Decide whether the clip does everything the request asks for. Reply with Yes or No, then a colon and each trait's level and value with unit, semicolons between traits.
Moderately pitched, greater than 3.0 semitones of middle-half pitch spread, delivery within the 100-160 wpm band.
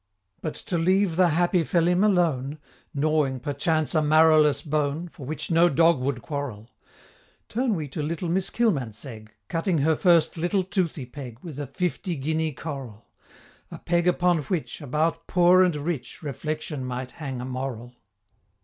Yes: medium, 155 Hz; average, 4.0 semitones; average, 155 wpm